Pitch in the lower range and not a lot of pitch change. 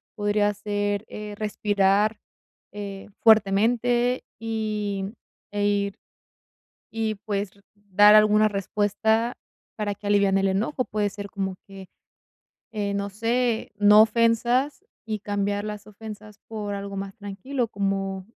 No: high, 205 Hz; narrow, 1.5 semitones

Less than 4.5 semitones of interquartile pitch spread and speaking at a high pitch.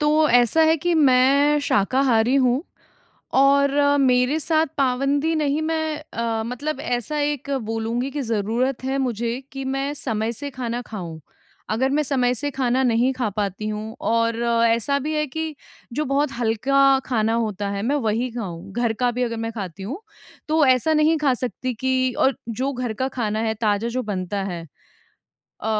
Yes: average, 3.8 semitones; very high, 250 Hz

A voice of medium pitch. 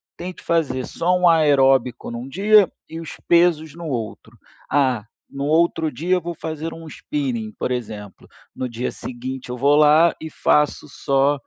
Yes: medium, 150 Hz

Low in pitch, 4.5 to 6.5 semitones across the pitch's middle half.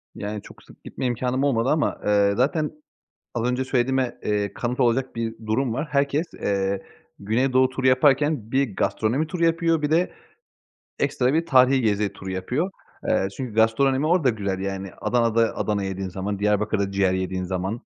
Yes: low, 120 Hz; average, 5.0 semitones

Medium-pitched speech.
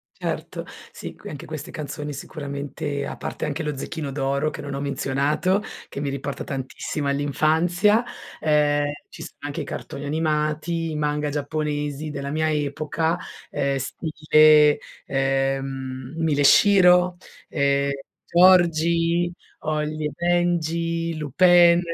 Yes: medium, 150 Hz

